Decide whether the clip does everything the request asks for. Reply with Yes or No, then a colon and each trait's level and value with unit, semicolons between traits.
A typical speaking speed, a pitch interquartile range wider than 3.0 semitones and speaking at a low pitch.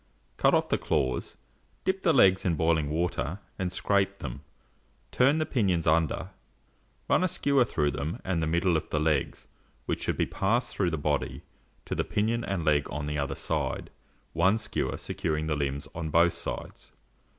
Yes: average, 180 wpm; average, 4.8 semitones; very low, 85 Hz